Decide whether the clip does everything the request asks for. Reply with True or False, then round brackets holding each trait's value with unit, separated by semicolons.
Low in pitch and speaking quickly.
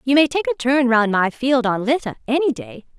False (255 Hz; 240 wpm)